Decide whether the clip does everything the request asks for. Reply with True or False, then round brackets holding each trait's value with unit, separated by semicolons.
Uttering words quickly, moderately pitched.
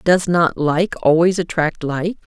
False (155 wpm; 170 Hz)